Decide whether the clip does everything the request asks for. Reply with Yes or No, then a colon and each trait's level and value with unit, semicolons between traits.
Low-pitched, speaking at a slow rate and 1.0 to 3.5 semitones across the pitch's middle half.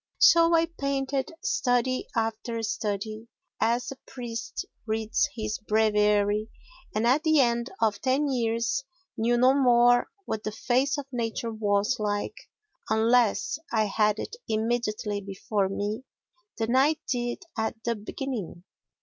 No: high, 230 Hz; slow, 130 wpm; average, 3.2 semitones